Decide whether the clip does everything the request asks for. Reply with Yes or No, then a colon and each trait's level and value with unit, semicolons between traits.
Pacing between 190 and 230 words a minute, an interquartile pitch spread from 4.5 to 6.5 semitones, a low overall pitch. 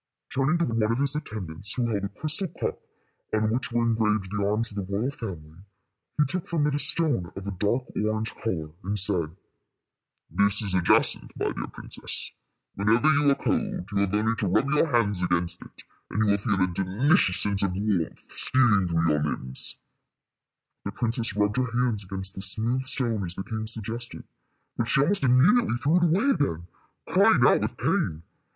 Yes: average, 195 wpm; average, 4.8 semitones; low, 110 Hz